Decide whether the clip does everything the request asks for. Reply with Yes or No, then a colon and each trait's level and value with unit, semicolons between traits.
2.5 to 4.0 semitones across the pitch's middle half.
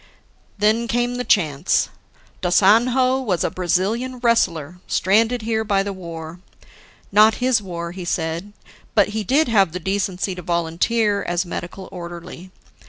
No: average, 4.7 semitones